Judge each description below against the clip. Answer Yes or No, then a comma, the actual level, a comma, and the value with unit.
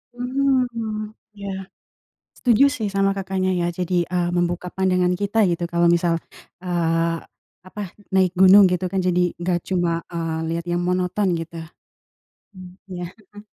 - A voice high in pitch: No, medium, 180 Hz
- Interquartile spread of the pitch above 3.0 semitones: No, narrow, 2.4 semitones